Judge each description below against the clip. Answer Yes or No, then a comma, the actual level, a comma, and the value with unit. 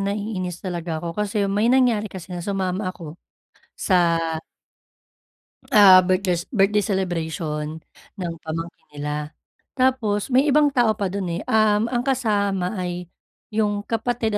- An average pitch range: Yes, average, 3.7 semitones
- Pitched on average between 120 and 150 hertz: No, high, 195 Hz